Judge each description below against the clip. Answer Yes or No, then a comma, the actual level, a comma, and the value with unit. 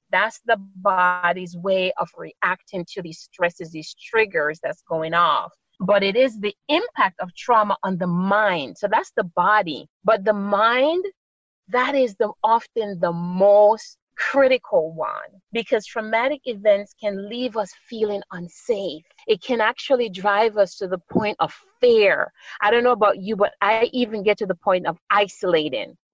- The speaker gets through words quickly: No, average, 165 wpm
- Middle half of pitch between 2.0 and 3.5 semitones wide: No, average, 4.3 semitones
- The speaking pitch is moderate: No, high, 210 Hz